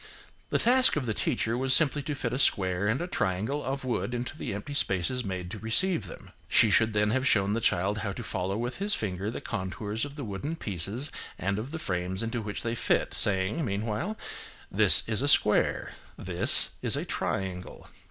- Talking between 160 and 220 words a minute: Yes, average, 200 wpm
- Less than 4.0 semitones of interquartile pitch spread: No, wide, 5.4 semitones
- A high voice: No, low, 110 Hz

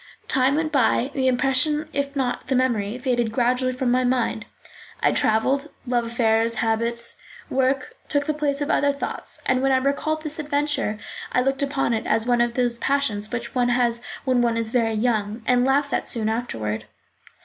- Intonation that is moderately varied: Yes, average, 3.1 semitones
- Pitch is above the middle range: Yes, very high, 250 Hz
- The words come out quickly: No, average, 185 wpm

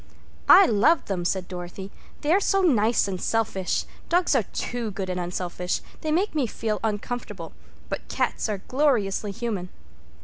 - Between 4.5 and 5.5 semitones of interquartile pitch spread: Yes, average, 5.1 semitones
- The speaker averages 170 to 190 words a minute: No, average, 160 wpm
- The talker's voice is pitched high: Yes, high, 210 Hz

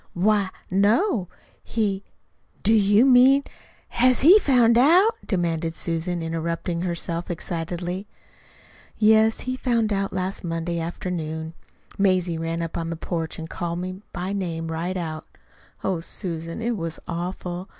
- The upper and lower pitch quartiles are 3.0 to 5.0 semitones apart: Yes, average, 4.2 semitones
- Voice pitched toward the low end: No, medium, 180 Hz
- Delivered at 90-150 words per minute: Yes, average, 140 wpm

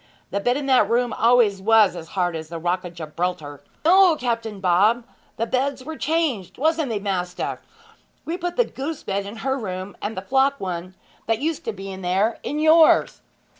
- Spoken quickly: No, average, 190 wpm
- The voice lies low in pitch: No, high, 225 Hz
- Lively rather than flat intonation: Yes, wide, 6.6 semitones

